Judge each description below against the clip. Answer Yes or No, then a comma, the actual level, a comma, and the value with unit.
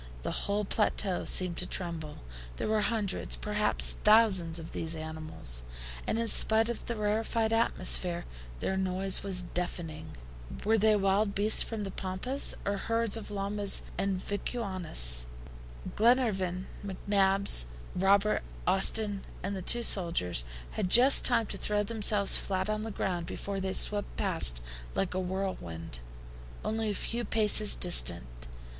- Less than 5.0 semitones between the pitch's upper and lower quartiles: Yes, average, 3.0 semitones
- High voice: Yes, high, 195 Hz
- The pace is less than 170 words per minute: Yes, average, 140 wpm